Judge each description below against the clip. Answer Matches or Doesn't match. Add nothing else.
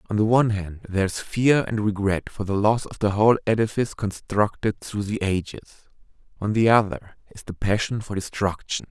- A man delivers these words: Matches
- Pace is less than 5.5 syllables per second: Doesn't match